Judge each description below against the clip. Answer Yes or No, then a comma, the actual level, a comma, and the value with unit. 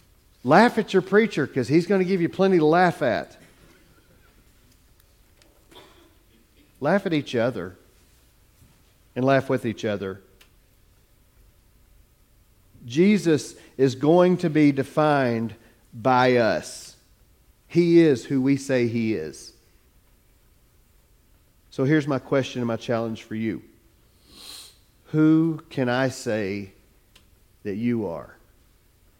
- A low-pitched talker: Yes, low, 120 Hz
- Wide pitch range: Yes, wide, 7.1 semitones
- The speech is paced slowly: Yes, slow, 110 wpm